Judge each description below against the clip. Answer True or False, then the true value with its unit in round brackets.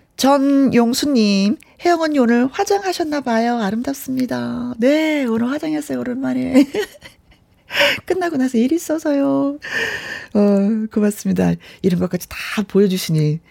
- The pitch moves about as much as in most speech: False (5.9 semitones)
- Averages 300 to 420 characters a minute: False (280 characters per minute)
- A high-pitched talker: True (255 Hz)